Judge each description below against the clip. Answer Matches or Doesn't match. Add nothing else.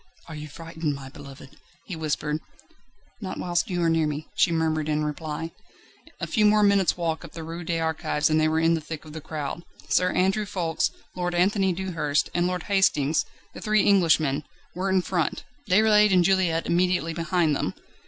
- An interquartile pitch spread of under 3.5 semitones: Matches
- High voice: Doesn't match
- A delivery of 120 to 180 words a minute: Doesn't match